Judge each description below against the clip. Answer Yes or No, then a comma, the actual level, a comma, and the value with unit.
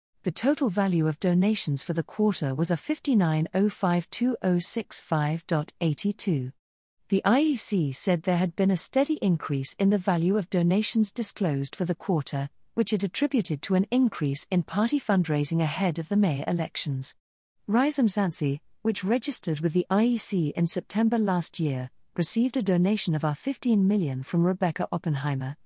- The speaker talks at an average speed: Yes, average, 150 wpm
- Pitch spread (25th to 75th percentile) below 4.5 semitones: No, average, 4.9 semitones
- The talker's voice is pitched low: No, medium, 180 Hz